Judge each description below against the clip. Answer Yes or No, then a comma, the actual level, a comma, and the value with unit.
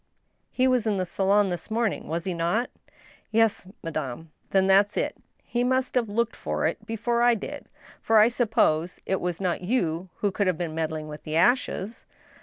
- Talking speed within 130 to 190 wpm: No, average, 200 wpm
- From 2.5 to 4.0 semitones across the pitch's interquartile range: No, average, 5.2 semitones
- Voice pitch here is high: Yes, high, 200 Hz